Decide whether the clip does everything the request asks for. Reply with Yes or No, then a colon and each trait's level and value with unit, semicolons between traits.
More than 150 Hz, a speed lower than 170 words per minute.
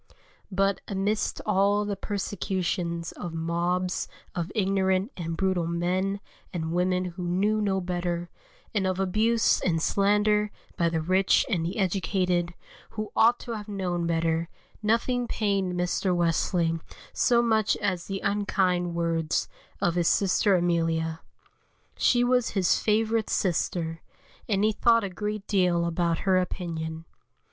Yes: medium, 185 Hz; slow, 135 wpm